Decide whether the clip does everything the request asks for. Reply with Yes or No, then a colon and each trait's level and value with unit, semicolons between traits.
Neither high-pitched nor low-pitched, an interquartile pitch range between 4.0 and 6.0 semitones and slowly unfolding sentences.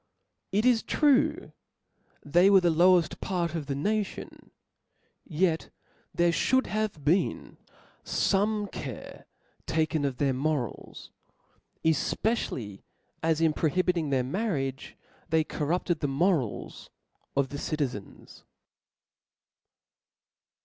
Yes: medium, 165 Hz; average, 5.2 semitones; slow, 100 wpm